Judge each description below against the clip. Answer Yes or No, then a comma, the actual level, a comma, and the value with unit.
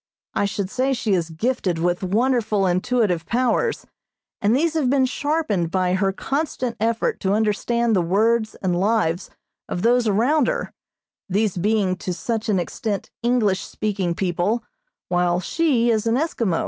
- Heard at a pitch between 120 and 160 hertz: No, high, 215 Hz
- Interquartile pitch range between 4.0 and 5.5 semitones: Yes, average, 4.5 semitones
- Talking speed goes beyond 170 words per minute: No, average, 155 wpm